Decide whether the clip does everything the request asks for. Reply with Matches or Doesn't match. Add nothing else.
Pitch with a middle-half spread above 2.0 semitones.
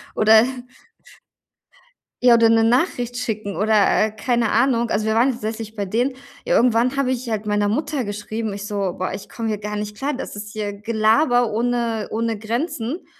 Matches